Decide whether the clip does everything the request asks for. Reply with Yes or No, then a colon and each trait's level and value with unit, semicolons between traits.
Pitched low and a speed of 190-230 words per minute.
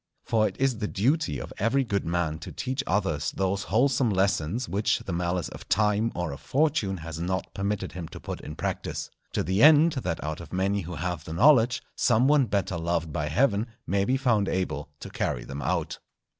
Yes: low, 100 Hz; fast, 205 wpm